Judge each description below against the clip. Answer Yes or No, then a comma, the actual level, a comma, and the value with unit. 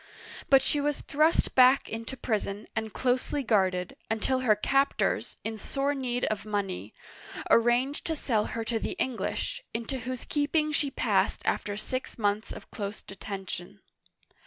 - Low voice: No, high, 235 Hz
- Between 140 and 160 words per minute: Yes, average, 150 wpm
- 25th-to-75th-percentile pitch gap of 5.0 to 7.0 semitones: No, average, 4.4 semitones